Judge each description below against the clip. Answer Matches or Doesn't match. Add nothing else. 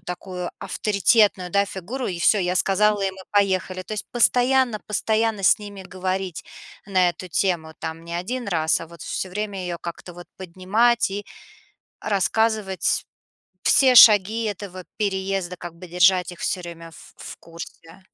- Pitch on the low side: Doesn't match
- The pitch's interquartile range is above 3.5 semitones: Doesn't match